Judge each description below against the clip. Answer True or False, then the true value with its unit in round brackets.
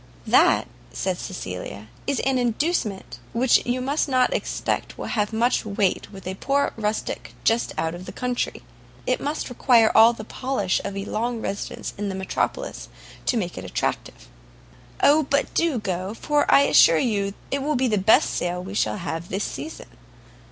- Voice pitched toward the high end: True (220 Hz)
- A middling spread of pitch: True (5.0 semitones)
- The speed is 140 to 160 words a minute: False (175 wpm)